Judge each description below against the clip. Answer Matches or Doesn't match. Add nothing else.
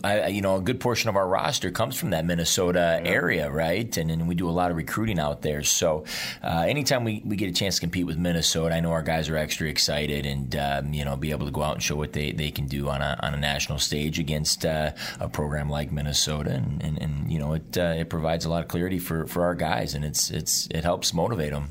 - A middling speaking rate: Doesn't match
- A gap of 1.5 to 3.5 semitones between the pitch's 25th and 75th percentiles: Matches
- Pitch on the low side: Matches